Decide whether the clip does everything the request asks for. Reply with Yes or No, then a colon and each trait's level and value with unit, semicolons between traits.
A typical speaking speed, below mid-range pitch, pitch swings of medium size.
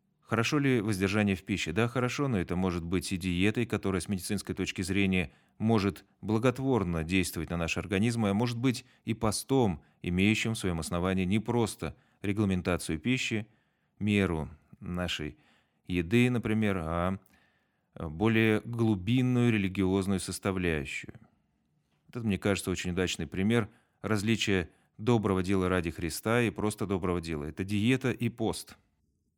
Yes: average, 135 wpm; low, 100 Hz; average, 3.7 semitones